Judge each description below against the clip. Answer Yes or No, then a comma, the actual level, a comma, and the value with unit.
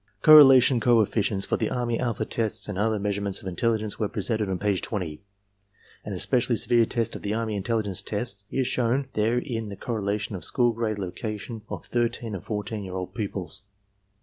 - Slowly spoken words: No, average, 180 wpm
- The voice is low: Yes, low, 110 Hz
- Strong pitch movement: No, average, 2.8 semitones